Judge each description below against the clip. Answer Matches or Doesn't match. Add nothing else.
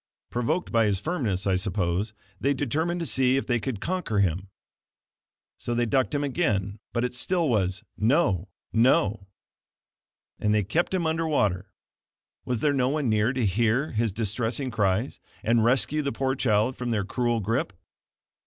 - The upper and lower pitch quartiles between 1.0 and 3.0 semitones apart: Doesn't match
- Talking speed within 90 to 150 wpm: Doesn't match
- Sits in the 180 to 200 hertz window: Doesn't match